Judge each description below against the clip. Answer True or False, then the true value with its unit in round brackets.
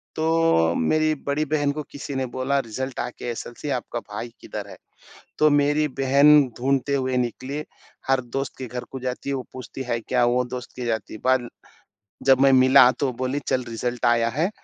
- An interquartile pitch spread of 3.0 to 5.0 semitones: False (2.4 semitones)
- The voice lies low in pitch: True (130 Hz)